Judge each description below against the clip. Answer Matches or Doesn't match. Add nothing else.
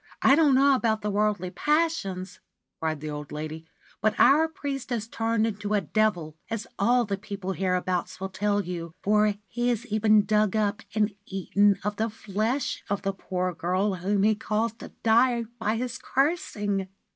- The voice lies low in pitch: Doesn't match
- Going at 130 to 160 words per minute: Doesn't match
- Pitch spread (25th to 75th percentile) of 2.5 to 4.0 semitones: Matches